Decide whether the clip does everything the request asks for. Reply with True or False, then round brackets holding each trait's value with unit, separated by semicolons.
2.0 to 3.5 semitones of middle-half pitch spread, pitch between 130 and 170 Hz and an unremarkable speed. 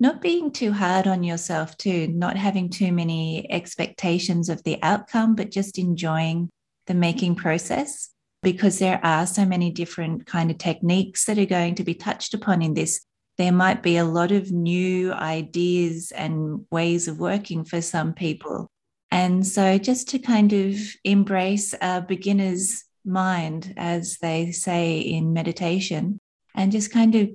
False (2.9 semitones; 180 Hz; 160 wpm)